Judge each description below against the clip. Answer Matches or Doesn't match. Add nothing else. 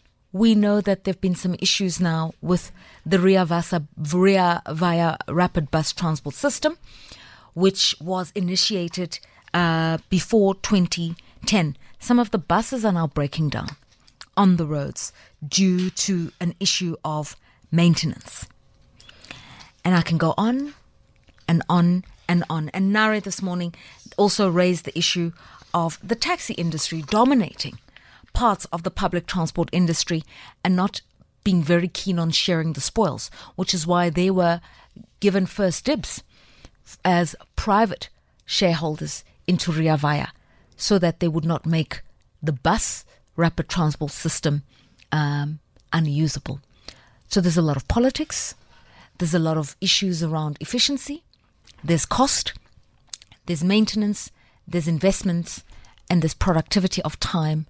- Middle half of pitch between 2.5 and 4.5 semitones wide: Matches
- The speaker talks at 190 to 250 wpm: Doesn't match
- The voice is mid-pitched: Matches